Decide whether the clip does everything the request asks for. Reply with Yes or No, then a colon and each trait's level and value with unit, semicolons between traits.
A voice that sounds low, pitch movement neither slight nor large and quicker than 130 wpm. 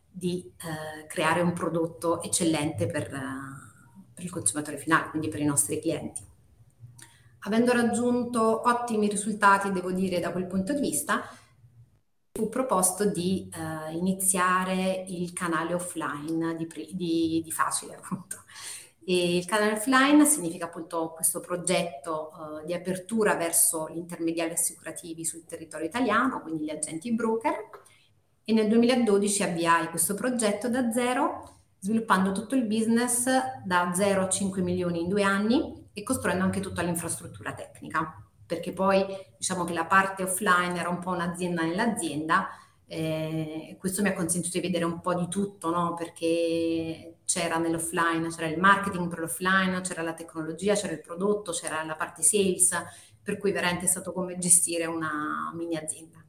No: medium, 175 Hz; average, 3.2 semitones; average, 150 wpm